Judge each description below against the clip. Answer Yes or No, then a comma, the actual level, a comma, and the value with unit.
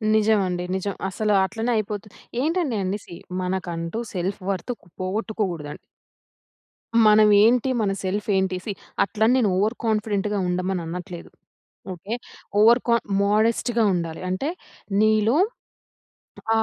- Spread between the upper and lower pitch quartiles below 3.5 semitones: Yes, average, 3.0 semitones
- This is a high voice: Yes, high, 205 Hz